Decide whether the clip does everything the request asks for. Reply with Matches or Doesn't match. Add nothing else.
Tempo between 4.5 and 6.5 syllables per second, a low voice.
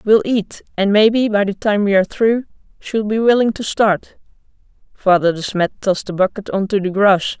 Doesn't match